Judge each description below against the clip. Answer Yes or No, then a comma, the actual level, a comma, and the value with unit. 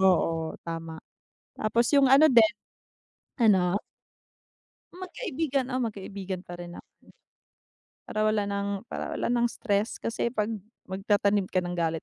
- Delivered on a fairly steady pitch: No, average, 4.5 semitones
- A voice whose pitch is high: Yes, high, 200 Hz